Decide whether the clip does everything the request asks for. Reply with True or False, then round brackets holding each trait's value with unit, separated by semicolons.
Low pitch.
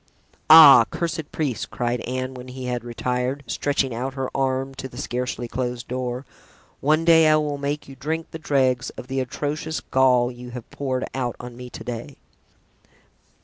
True (130 Hz)